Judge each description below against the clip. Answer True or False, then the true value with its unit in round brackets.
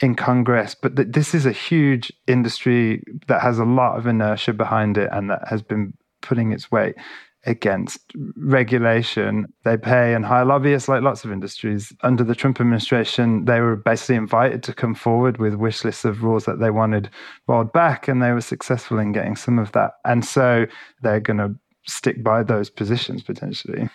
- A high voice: False (115 Hz)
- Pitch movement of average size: False (2.3 semitones)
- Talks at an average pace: True (190 wpm)